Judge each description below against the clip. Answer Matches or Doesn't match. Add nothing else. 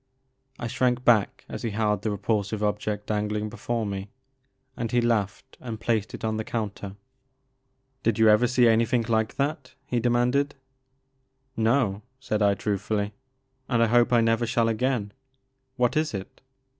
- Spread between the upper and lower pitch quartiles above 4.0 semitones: Doesn't match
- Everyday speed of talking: Matches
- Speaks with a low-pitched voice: Matches